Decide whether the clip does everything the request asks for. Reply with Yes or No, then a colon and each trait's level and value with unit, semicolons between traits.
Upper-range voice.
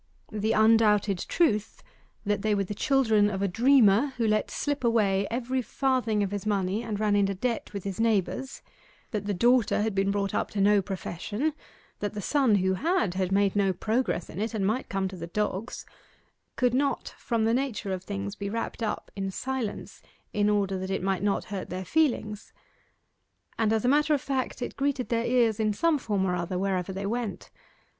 Yes: high, 210 Hz